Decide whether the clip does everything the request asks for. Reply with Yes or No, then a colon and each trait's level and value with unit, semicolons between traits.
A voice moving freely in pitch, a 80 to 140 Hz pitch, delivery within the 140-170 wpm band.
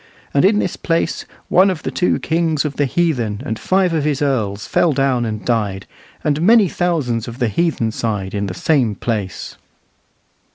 No: wide, 7.0 semitones; low, 135 Hz; average, 180 wpm